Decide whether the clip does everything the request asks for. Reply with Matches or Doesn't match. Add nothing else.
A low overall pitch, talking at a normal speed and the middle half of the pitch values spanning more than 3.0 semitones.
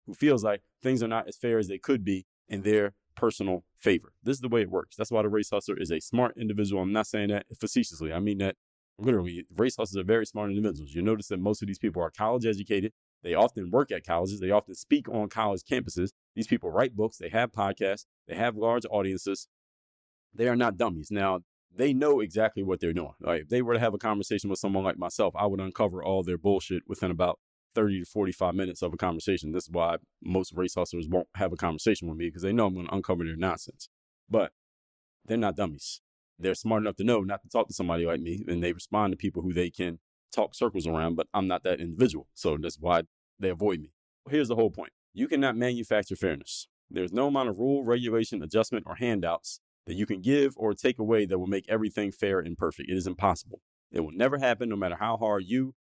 Doesn't match